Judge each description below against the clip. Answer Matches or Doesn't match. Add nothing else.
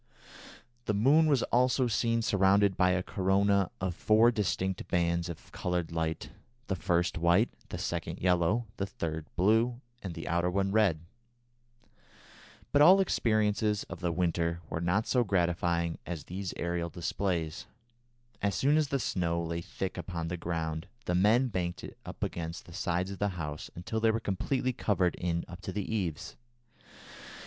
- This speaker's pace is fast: Doesn't match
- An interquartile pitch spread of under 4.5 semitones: Matches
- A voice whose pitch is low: Matches